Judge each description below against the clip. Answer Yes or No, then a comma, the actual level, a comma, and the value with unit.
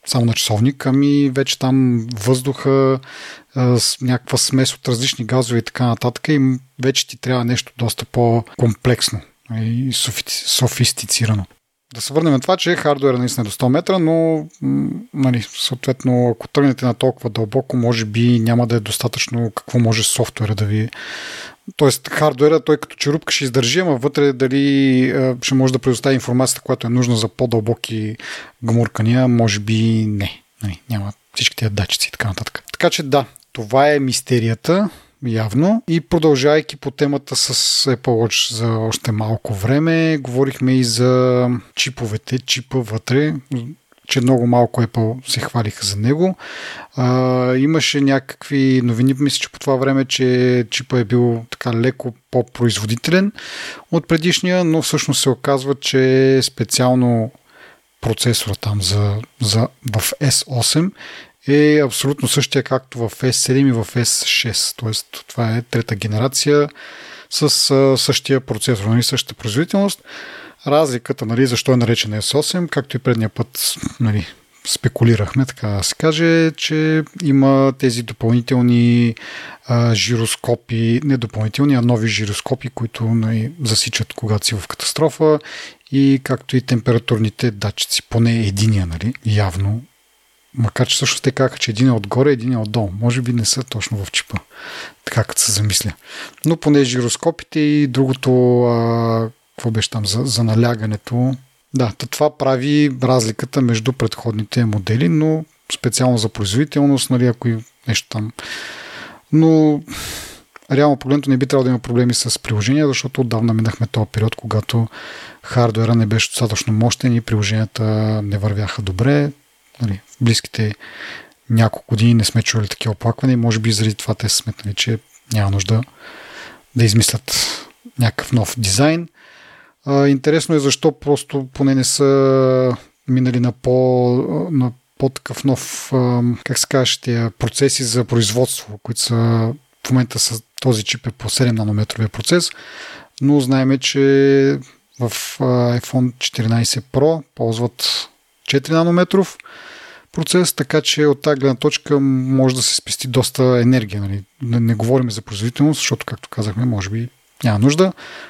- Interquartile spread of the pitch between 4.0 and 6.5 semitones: No, average, 3.3 semitones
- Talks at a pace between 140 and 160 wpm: Yes, average, 145 wpm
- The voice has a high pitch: No, low, 125 Hz